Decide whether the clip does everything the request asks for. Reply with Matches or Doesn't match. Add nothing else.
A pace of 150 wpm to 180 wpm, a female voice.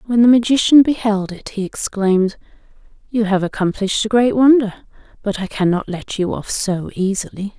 Matches